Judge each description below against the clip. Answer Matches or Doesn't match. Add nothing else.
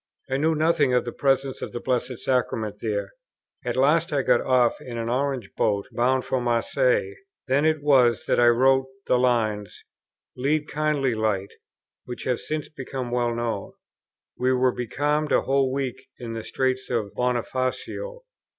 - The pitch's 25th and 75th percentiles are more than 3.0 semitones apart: Doesn't match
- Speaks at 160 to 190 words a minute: Matches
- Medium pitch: Doesn't match